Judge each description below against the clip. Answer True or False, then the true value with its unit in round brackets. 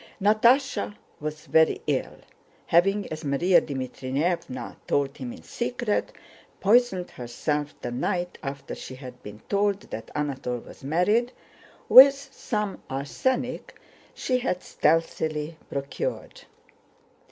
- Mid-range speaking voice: True (165 Hz)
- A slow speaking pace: True (110 wpm)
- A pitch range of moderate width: False (7.3 semitones)